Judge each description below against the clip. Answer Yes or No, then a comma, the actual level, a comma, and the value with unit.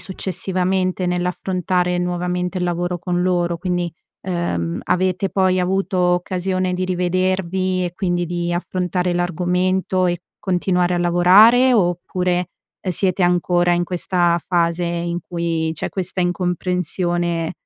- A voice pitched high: No, medium, 180 Hz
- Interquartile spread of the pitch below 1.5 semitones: Yes, narrow, 1.0 semitones